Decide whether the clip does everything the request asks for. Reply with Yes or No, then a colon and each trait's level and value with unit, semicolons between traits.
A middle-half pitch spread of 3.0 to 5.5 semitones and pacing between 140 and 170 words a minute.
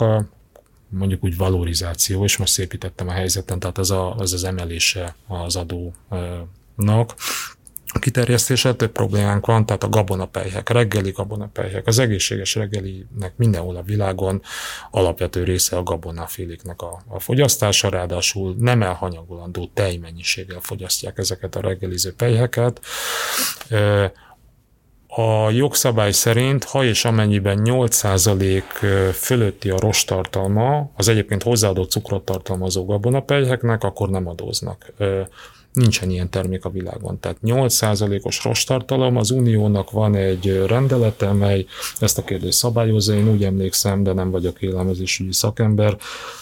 No: average, 3.4 semitones; average, 125 wpm